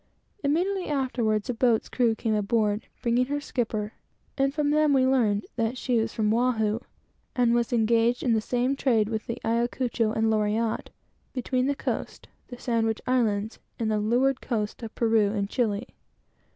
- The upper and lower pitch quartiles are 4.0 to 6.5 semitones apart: No, narrow, 2.6 semitones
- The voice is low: No, high, 230 Hz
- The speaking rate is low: No, average, 165 wpm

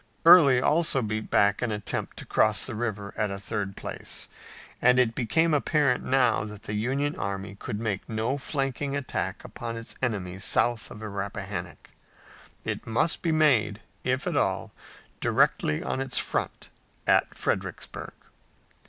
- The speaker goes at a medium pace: Yes, average, 155 wpm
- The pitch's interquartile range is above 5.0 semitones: No, average, 4.5 semitones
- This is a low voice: Yes, low, 115 Hz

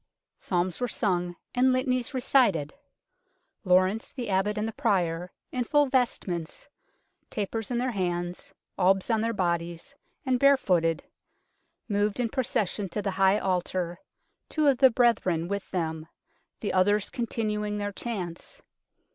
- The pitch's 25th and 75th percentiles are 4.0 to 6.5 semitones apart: Yes, average, 5.0 semitones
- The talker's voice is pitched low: No, high, 205 Hz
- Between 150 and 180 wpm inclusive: No, average, 140 wpm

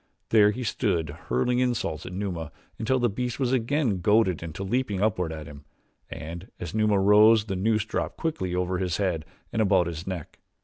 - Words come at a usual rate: Yes, average, 185 wpm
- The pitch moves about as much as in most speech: Yes, average, 4.2 semitones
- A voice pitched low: Yes, low, 100 Hz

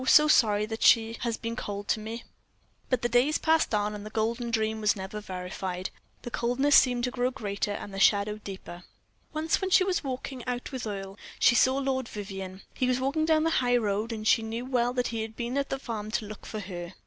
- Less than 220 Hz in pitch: No, high, 230 Hz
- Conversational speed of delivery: No, fast, 230 wpm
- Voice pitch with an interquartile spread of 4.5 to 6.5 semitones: No, average, 3.6 semitones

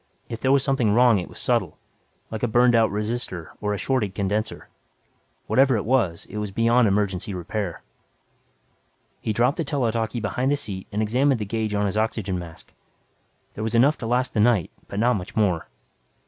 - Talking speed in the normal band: Yes, average, 190 wpm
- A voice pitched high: No, low, 110 Hz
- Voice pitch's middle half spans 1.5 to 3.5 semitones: Yes, average, 3.2 semitones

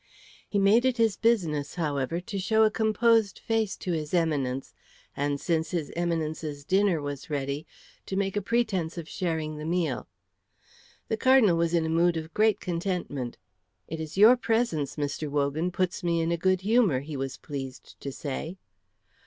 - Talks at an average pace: Yes, average, 170 wpm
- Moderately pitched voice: Yes, medium, 170 Hz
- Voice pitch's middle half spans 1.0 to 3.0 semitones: No, average, 5.0 semitones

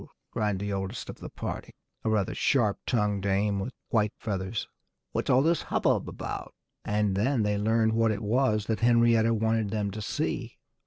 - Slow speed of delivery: No, average, 175 wpm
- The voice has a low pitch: Yes, low, 110 Hz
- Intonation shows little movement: Yes, narrow, 2.0 semitones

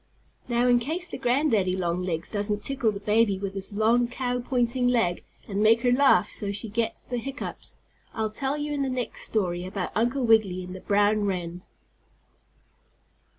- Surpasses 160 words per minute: Yes, average, 175 wpm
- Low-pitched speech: No, high, 220 Hz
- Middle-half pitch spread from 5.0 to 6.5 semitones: No, average, 4.0 semitones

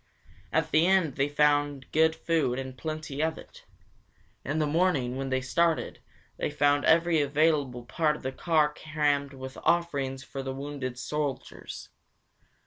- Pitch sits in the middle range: Yes, medium, 145 Hz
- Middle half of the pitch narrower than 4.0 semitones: Yes, average, 2.9 semitones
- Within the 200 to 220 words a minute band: No, average, 150 wpm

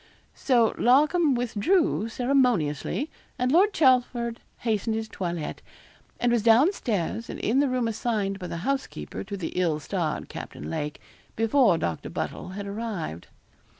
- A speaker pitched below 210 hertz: No, high, 225 Hz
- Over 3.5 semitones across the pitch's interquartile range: Yes, average, 5.2 semitones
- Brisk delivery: No, average, 145 wpm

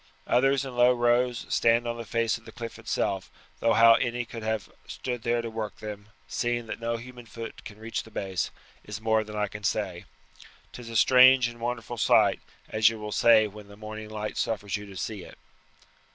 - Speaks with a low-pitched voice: Yes, low, 115 Hz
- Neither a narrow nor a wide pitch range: No, narrow, 2.0 semitones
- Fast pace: Yes, fast, 210 wpm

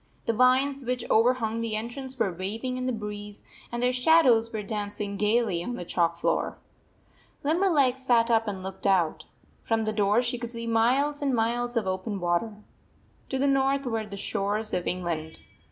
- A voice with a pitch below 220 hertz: No, high, 225 Hz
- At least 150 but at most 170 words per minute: No, average, 180 wpm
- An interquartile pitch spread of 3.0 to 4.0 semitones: Yes, average, 3.7 semitones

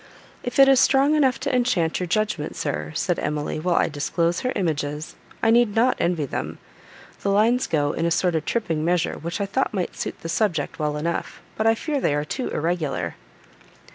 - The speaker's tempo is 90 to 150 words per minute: No, average, 200 wpm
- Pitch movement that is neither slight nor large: No, wide, 6.6 semitones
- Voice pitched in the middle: Yes, medium, 175 Hz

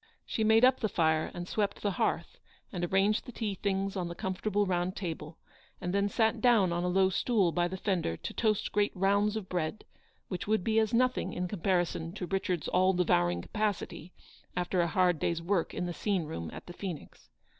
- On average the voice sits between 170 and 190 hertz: Yes, medium, 185 Hz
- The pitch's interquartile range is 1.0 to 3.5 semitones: Yes, average, 2.9 semitones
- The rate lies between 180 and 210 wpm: Yes, fast, 205 wpm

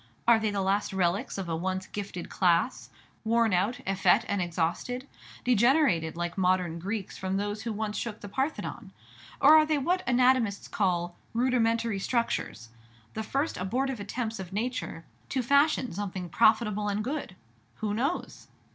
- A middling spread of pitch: Yes, average, 4.7 semitones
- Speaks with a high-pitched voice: Yes, high, 210 Hz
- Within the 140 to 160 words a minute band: Yes, average, 155 wpm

